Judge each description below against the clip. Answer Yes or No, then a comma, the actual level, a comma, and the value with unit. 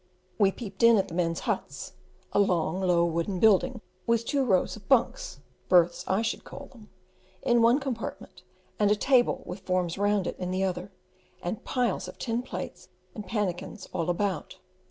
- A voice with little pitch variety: No, average, 4.2 semitones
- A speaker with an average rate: Yes, average, 175 wpm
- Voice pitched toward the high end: Yes, high, 200 Hz